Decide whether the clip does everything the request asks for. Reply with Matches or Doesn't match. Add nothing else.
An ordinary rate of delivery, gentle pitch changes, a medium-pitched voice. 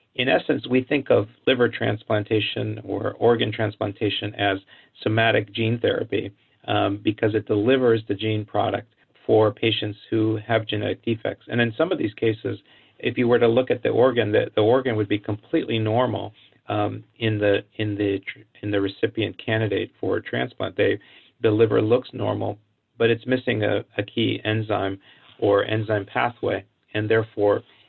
Doesn't match